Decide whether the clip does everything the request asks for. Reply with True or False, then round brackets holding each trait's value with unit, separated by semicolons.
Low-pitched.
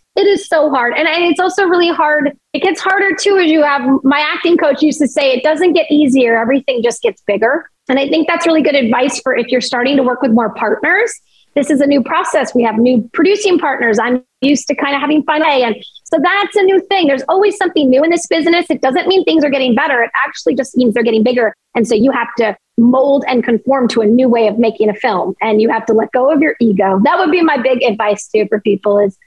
False (275 Hz)